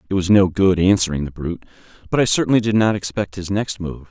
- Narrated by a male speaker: Yes, male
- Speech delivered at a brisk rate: Yes, fast, 235 wpm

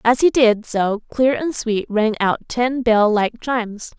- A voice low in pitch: No, high, 230 Hz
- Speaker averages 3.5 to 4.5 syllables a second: Yes, 4.0 syllables/s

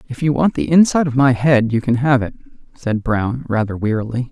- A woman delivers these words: No, male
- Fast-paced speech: Yes, fast, 220 wpm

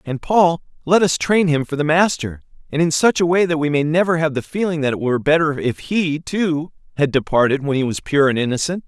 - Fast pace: Yes, fast, 245 wpm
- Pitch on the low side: No, medium, 155 Hz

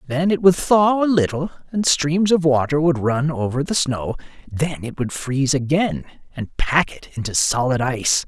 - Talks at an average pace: Yes, average, 190 wpm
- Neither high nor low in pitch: Yes, medium, 150 Hz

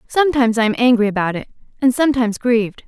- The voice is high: Yes, high, 235 Hz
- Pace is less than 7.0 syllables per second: No, 7.5 syllables/s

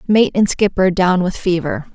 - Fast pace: No, average, 185 wpm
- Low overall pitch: No, high, 190 Hz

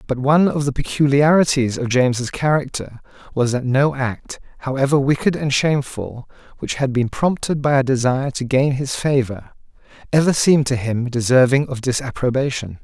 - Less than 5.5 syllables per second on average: Yes, 5.3 syllables/s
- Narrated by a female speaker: No, male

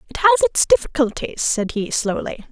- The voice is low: No, very high, 285 Hz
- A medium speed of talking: Yes, average, 165 wpm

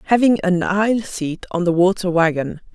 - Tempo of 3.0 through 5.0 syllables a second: Yes, 4.9 syllables/s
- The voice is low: No, medium, 185 Hz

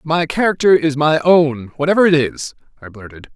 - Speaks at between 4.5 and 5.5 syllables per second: Yes, 5.3 syllables/s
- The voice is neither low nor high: Yes, medium, 150 Hz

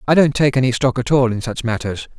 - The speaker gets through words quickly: Yes, fast, 275 wpm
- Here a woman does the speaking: No, male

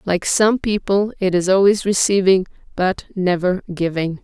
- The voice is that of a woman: Yes, female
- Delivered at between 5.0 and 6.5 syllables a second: No, 4.5 syllables/s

